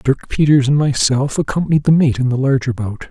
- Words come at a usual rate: No, fast, 215 wpm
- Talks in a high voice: No, low, 135 Hz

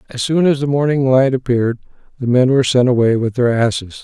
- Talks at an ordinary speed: No, fast, 225 wpm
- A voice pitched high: No, low, 130 Hz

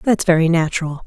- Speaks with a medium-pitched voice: Yes, medium, 170 Hz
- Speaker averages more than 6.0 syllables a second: Yes, 6.3 syllables/s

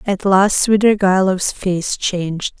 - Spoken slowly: Yes, slow, 115 wpm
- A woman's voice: Yes, female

